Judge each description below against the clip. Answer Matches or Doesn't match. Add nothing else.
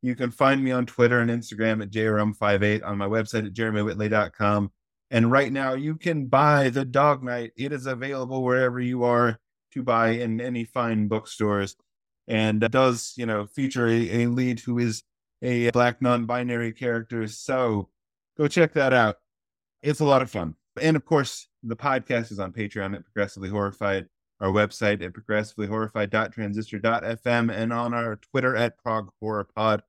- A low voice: Matches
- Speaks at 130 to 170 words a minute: Matches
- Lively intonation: Doesn't match